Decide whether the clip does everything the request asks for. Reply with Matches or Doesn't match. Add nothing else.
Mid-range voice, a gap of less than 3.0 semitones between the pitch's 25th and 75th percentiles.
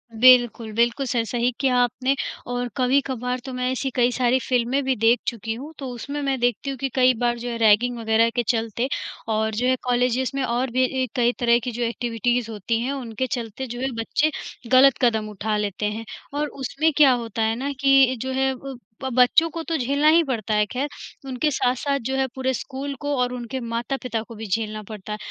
Doesn't match